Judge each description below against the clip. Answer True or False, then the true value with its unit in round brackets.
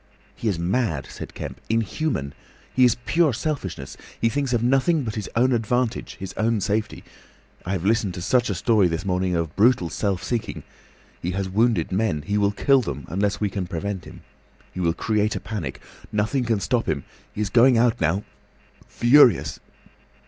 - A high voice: False (105 Hz)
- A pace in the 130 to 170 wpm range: False (180 wpm)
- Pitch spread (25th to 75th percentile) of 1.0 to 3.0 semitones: False (4.6 semitones)